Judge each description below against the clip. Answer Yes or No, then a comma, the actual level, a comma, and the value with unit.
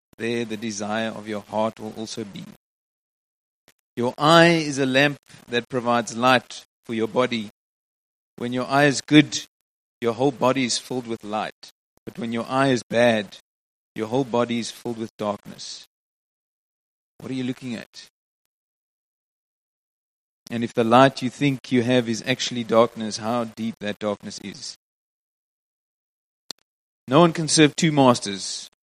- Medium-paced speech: Yes, average, 150 wpm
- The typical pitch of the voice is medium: No, low, 120 Hz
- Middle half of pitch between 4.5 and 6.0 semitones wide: No, average, 2.7 semitones